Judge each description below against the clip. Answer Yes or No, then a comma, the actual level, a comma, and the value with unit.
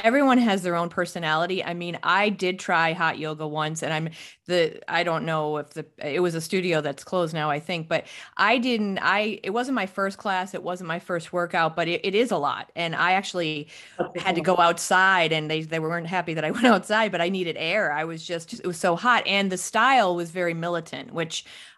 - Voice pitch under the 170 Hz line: No, medium, 175 Hz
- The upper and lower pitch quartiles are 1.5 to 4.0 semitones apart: Yes, average, 2.8 semitones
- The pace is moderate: No, fast, 230 wpm